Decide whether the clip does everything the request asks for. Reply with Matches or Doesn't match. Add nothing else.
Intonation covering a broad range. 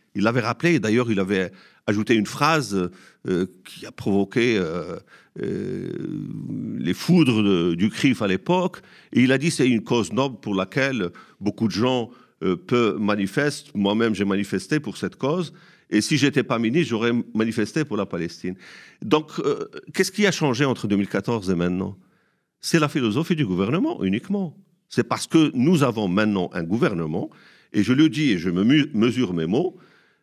Matches